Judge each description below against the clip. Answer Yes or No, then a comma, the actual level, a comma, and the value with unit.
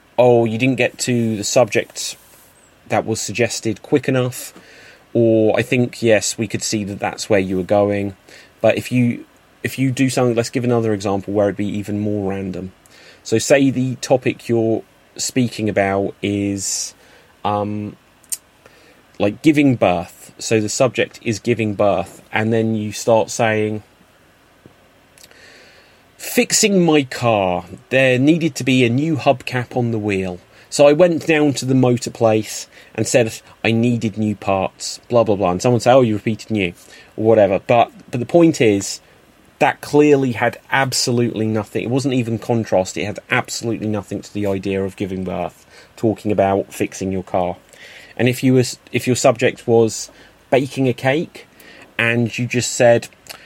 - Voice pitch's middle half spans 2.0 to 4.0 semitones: Yes, average, 3.6 semitones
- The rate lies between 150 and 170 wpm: Yes, average, 165 wpm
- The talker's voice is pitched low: Yes, low, 115 Hz